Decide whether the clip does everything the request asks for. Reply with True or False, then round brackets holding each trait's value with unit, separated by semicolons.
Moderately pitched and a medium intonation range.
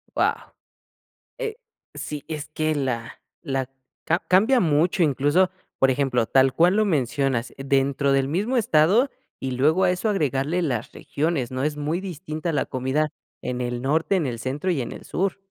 True (150 Hz; 5.0 semitones)